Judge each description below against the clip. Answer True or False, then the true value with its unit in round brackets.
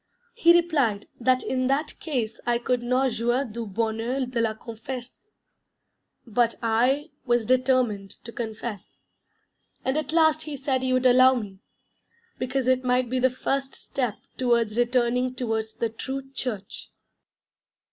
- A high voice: True (250 Hz)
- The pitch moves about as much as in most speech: False (2.3 semitones)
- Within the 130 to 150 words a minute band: True (145 wpm)